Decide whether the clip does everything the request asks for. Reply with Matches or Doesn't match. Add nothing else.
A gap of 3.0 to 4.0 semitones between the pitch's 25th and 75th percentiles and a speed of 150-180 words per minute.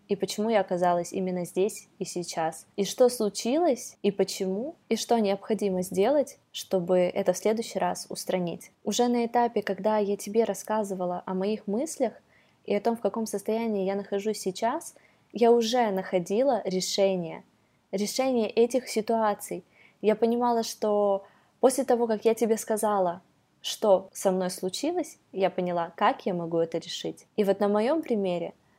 Matches